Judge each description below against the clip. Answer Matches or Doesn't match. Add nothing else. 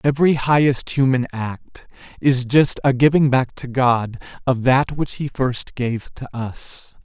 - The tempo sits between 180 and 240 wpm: Doesn't match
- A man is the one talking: Matches